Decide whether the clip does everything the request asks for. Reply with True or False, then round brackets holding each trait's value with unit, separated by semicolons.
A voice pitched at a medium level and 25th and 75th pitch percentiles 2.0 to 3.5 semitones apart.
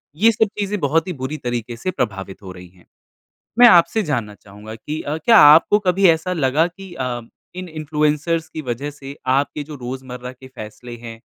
False (145 Hz; 5.5 semitones)